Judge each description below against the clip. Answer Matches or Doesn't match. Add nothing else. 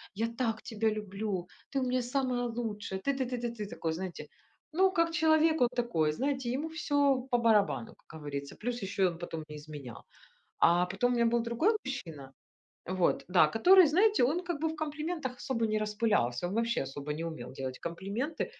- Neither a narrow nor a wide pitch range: Doesn't match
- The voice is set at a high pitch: Matches